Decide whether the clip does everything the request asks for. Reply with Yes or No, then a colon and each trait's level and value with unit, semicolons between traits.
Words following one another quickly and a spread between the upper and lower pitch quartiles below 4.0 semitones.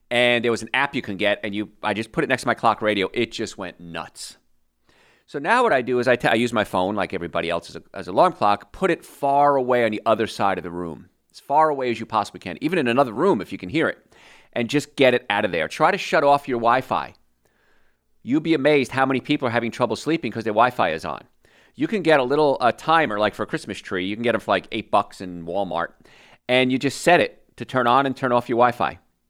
No: fast, 275 wpm; average, 4.4 semitones